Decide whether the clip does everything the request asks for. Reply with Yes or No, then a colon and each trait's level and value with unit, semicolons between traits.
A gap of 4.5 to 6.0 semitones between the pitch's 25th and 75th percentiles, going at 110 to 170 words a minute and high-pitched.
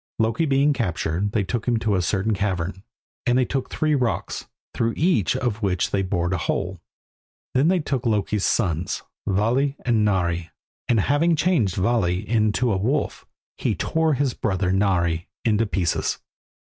No: average, 5.2 semitones; average, 160 wpm; low, 105 Hz